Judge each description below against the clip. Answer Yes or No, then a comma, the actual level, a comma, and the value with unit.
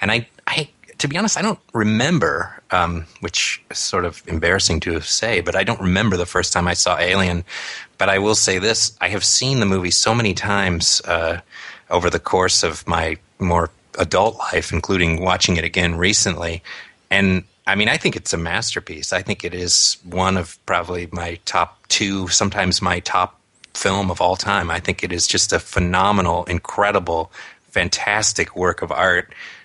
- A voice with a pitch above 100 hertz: No, very low, 95 Hz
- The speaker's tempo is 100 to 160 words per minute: No, average, 185 wpm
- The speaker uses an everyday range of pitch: Yes, average, 3.0 semitones